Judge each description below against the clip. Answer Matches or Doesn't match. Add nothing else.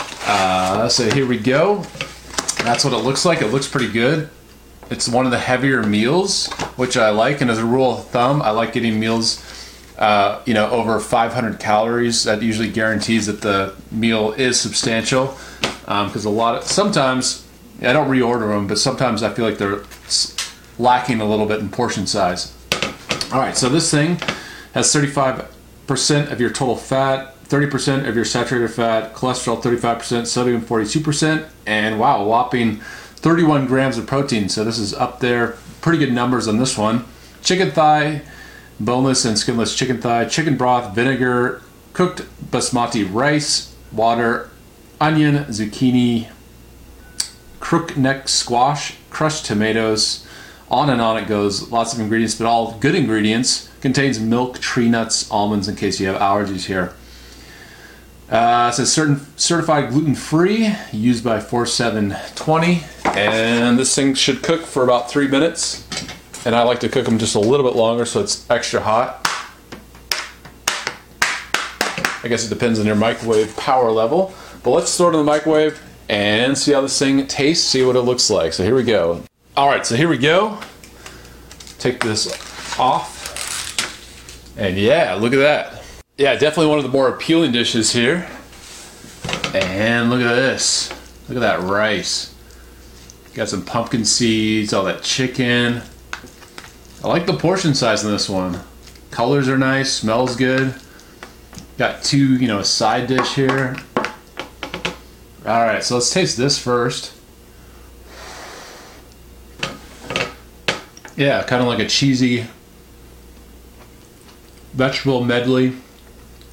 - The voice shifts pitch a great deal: Doesn't match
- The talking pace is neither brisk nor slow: Matches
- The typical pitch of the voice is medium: Doesn't match